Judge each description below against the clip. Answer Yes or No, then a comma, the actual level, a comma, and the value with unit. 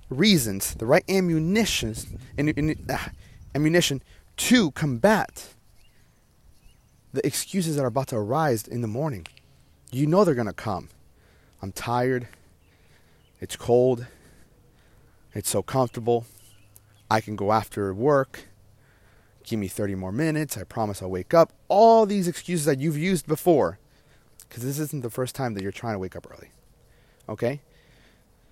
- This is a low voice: Yes, low, 120 Hz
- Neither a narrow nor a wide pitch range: No, wide, 6.8 semitones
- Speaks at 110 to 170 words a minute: Yes, average, 140 wpm